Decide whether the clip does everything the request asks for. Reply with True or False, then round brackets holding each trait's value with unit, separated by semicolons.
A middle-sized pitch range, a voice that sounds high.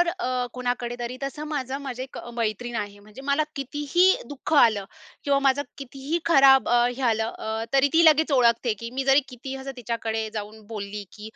True (3.4 semitones; 250 Hz)